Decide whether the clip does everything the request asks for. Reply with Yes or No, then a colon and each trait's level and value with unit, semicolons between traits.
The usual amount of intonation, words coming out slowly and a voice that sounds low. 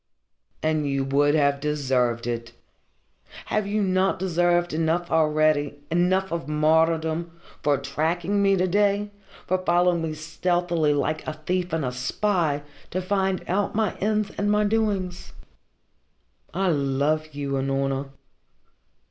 No: average, 4.2 semitones; slow, 130 wpm; medium, 165 Hz